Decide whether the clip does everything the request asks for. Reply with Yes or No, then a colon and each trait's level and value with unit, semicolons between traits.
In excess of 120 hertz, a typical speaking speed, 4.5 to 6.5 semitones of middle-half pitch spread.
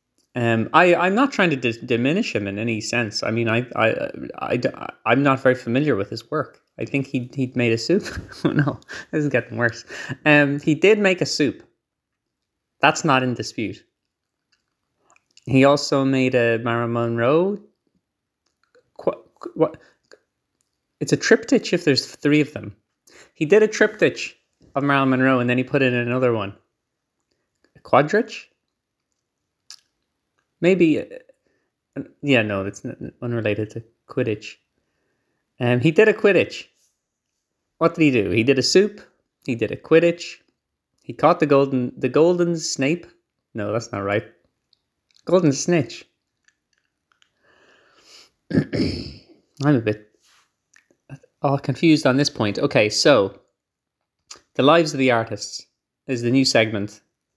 Yes: low, 135 Hz; average, 145 wpm; wide, 5.5 semitones